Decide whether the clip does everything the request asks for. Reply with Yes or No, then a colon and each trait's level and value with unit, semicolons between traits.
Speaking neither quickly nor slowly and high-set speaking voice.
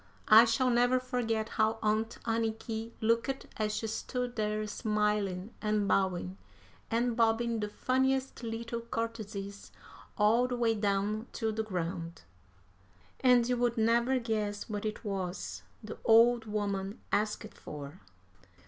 No: slow, 130 wpm; high, 220 Hz